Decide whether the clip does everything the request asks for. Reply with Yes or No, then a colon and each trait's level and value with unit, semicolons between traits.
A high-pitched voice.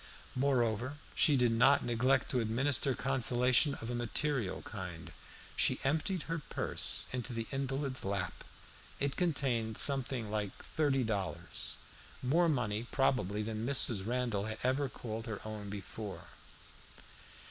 No: low, 120 Hz